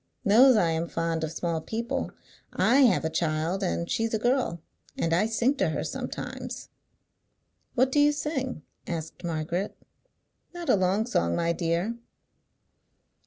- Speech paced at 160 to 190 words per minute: No, average, 150 wpm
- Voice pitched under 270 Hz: Yes, medium, 185 Hz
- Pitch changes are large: Yes, wide, 6.2 semitones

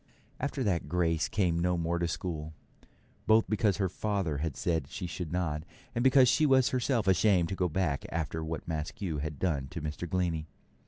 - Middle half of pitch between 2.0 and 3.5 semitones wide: No, average, 3.9 semitones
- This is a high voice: No, very low, 85 Hz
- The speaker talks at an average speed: Yes, average, 190 wpm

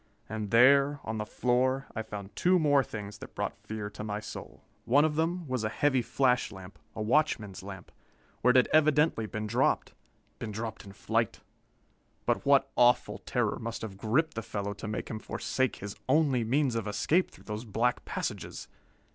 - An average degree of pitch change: Yes, average, 4.5 semitones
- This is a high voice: No, low, 115 Hz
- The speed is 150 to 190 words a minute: Yes, average, 185 wpm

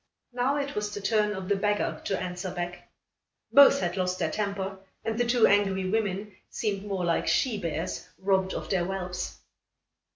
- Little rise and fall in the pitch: Yes, narrow, 2.2 semitones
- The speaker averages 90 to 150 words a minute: No, average, 175 wpm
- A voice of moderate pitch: No, high, 195 Hz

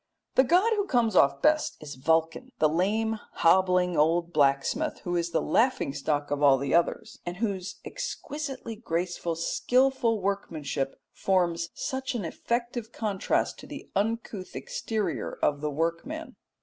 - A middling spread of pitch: No, wide, 6.5 semitones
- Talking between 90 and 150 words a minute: Yes, average, 145 wpm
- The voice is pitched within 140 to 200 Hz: Yes, medium, 185 Hz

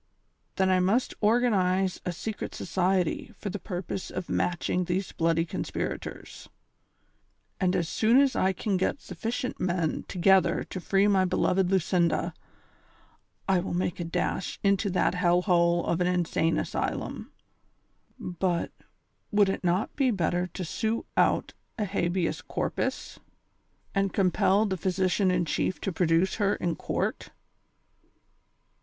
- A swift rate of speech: No, average, 145 wpm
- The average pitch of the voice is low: No, medium, 185 Hz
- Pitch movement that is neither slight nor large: No, narrow, 2.1 semitones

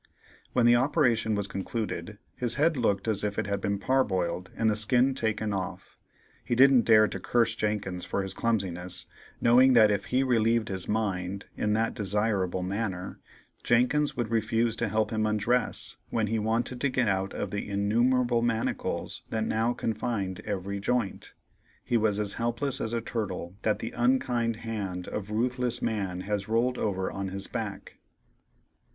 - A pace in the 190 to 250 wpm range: No, average, 170 wpm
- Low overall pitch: Yes, low, 110 Hz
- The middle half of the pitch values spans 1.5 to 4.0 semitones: Yes, average, 3.0 semitones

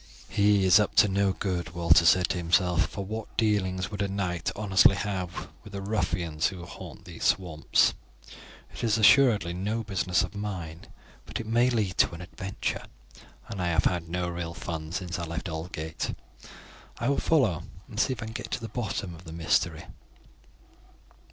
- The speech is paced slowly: No, average, 185 wpm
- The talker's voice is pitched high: No, very low, 95 Hz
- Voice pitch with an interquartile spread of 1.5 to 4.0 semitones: Yes, average, 3.3 semitones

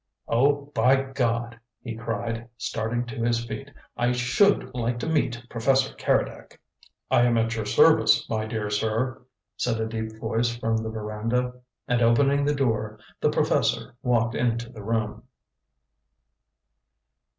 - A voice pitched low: Yes, low, 115 Hz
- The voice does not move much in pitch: Yes, narrow, 1.7 semitones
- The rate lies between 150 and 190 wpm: No, average, 140 wpm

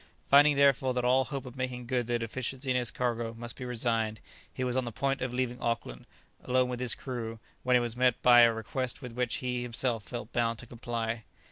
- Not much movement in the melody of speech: Yes, narrow, 1.6 semitones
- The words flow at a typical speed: No, fast, 225 wpm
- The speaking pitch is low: Yes, low, 125 Hz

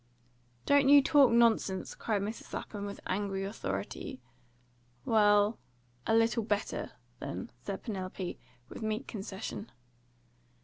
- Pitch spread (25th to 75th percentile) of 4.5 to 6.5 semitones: No, average, 2.7 semitones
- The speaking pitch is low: No, high, 210 Hz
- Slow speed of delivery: Yes, slow, 115 wpm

